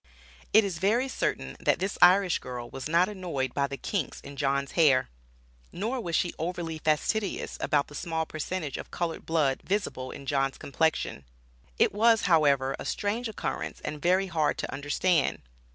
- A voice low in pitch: No, medium, 165 Hz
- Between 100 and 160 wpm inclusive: No, average, 170 wpm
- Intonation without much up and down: No, average, 5.2 semitones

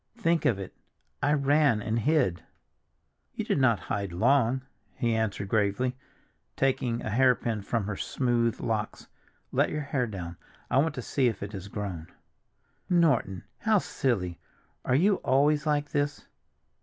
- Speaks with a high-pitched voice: No, low, 120 Hz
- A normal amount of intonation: No, wide, 5.8 semitones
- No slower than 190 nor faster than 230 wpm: No, average, 150 wpm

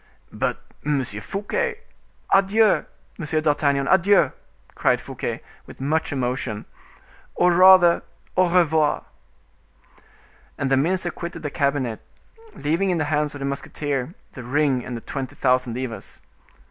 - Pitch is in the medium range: Yes, medium, 150 Hz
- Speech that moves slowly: Yes, slow, 130 wpm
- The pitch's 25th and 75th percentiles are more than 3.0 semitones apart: Yes, average, 4.6 semitones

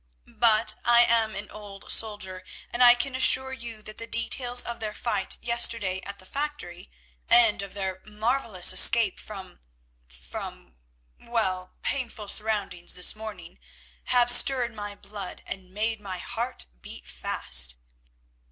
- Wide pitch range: No, average, 4.1 semitones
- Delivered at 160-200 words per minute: No, slow, 135 wpm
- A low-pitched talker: No, high, 210 Hz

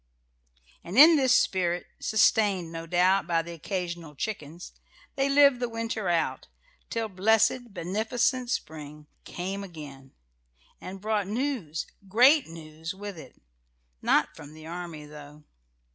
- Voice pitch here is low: No, medium, 185 Hz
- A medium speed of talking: No, slow, 130 wpm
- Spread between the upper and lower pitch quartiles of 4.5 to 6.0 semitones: Yes, wide, 5.5 semitones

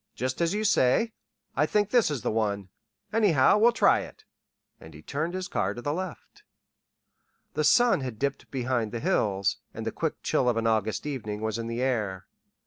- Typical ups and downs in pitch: No, wide, 7.3 semitones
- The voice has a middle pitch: No, low, 130 Hz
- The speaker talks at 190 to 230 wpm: Yes, average, 195 wpm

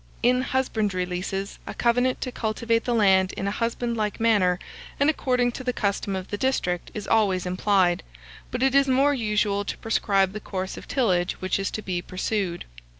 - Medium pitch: No, high, 210 Hz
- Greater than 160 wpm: Yes, average, 185 wpm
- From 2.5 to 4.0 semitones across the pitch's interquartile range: No, average, 4.4 semitones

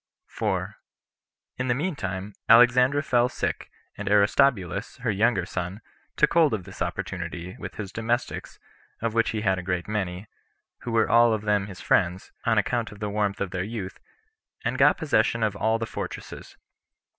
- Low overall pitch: Yes, low, 105 Hz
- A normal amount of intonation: Yes, average, 3.6 semitones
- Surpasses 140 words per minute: Yes, average, 175 wpm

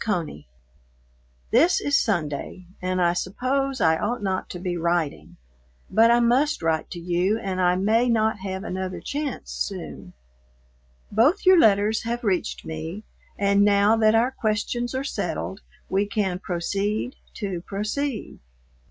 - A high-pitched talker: Yes, high, 205 Hz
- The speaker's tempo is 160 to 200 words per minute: No, average, 145 wpm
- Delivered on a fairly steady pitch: No, average, 4.6 semitones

